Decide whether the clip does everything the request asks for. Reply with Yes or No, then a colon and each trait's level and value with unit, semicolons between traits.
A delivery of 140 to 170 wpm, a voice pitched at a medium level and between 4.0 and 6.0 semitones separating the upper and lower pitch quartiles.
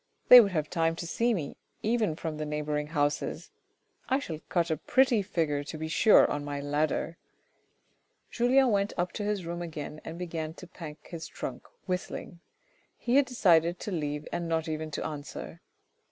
No: average, 180 wpm; medium, 165 Hz; average, 4.4 semitones